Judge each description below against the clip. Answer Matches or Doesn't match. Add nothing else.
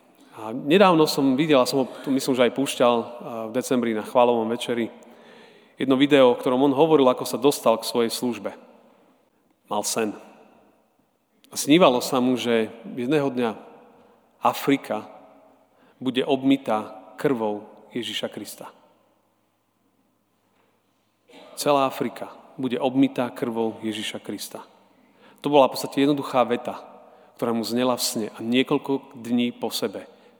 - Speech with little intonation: Doesn't match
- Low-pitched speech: Matches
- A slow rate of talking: Doesn't match